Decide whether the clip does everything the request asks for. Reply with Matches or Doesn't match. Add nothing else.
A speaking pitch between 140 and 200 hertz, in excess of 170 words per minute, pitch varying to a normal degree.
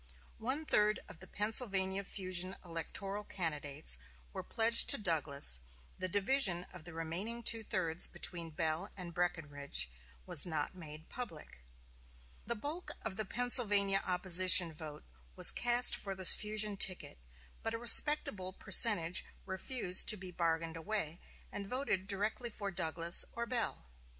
Doesn't match